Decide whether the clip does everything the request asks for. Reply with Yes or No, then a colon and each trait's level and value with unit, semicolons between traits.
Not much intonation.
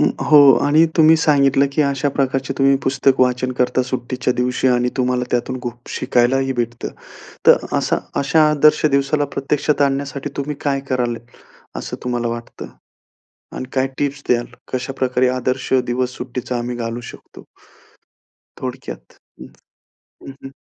Yes: narrow, 2.0 semitones